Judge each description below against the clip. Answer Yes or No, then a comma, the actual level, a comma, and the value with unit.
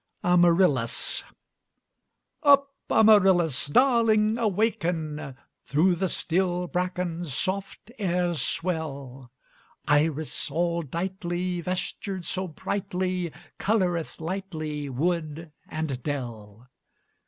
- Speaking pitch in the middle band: Yes, medium, 175 Hz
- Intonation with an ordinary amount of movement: Yes, average, 3.6 semitones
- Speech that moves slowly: Yes, slow, 80 wpm